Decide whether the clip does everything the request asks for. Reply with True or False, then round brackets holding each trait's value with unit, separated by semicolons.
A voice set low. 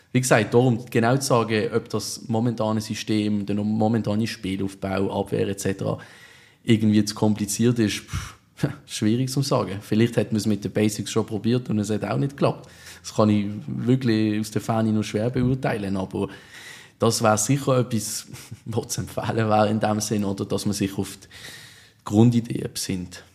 True (110 Hz)